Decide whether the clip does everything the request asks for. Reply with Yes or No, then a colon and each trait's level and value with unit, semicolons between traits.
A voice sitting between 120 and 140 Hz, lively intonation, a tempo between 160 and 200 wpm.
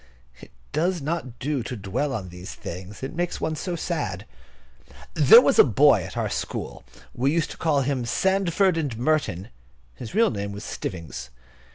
Yes: low, 135 Hz; wide, 8.1 semitones; average, 175 wpm